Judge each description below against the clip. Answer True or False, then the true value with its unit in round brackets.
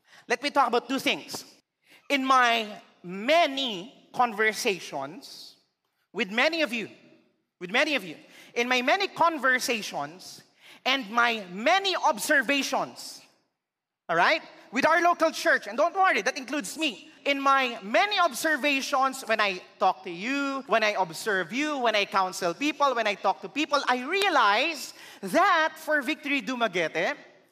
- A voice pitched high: True (270 Hz)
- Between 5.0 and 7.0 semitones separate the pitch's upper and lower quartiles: True (5.4 semitones)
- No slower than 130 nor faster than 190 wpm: True (145 wpm)